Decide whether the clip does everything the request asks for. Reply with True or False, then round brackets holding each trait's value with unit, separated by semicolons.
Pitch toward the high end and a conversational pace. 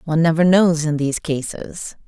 False (160 Hz; 175 wpm)